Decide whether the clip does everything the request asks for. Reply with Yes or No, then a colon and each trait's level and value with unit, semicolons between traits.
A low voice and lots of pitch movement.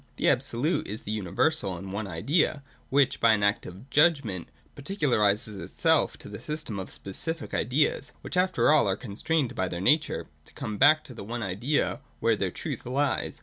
Yes: low, 120 Hz; wide, 7.1 semitones